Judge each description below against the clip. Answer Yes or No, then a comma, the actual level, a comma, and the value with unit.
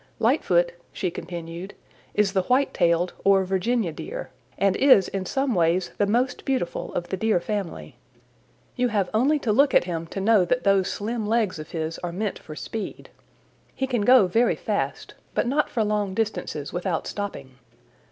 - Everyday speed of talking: Yes, average, 175 wpm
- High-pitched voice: Yes, high, 200 Hz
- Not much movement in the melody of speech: No, average, 5.1 semitones